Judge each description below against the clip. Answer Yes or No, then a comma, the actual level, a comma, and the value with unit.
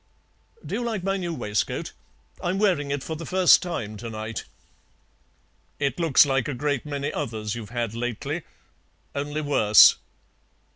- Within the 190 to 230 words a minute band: No, average, 150 wpm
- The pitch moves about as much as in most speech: No, wide, 6.3 semitones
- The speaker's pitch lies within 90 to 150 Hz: Yes, medium, 140 Hz